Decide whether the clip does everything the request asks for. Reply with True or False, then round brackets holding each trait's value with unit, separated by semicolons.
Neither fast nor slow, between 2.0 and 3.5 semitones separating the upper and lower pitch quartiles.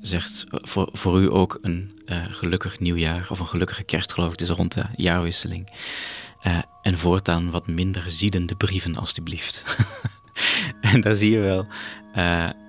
True (165 wpm; 3.2 semitones)